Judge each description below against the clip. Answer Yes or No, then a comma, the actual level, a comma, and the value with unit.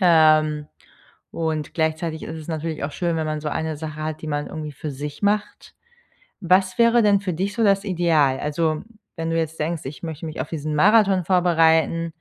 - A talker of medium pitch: Yes, medium, 160 Hz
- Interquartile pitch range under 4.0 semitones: Yes, narrow, 2.5 semitones